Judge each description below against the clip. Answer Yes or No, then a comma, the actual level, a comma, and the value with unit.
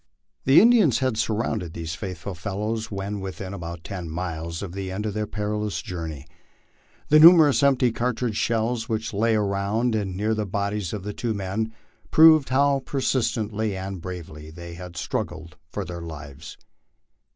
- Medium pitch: No, low, 105 Hz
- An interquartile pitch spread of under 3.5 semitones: No, average, 4.1 semitones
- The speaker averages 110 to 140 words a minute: No, average, 160 wpm